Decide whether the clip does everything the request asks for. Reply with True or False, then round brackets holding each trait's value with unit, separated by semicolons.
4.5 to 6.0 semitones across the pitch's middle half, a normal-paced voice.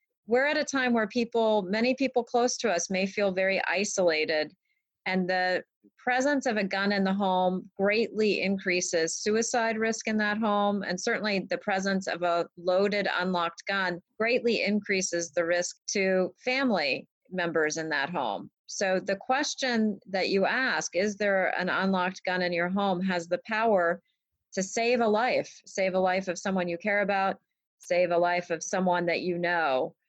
False (3.8 semitones; 175 wpm)